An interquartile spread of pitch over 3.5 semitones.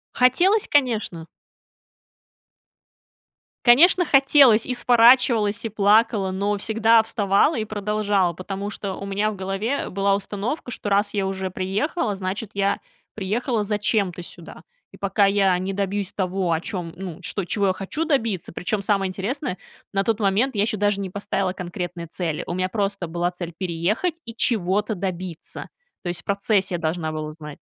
No: average, 3.0 semitones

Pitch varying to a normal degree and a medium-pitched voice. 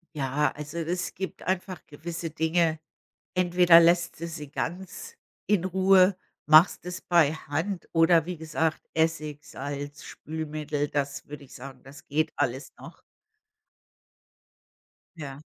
Yes: average, 3.1 semitones; medium, 160 Hz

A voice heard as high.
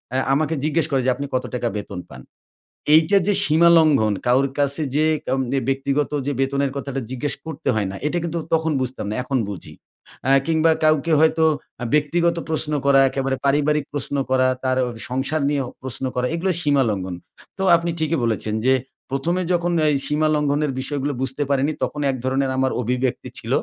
No: medium, 140 Hz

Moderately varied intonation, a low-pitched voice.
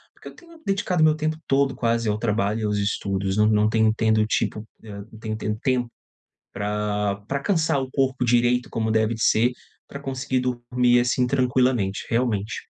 Yes: average, 3.4 semitones; low, 120 Hz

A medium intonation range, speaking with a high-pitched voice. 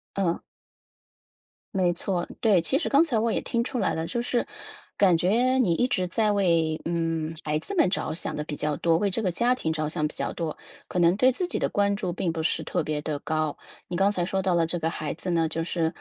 No: average, 4.2 semitones; medium, 175 Hz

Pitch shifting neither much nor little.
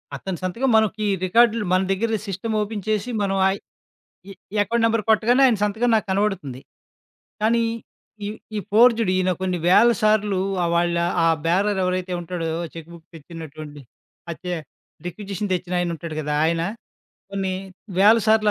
Yes: average, 3.7 semitones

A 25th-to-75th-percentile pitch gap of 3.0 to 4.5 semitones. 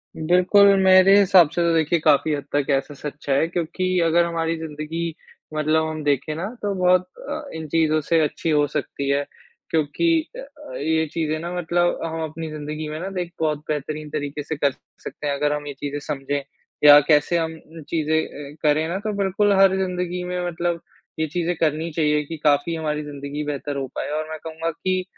No: narrow, 2.6 semitones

